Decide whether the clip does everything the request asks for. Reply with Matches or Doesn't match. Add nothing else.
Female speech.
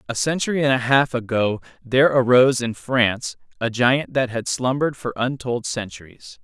Doesn't match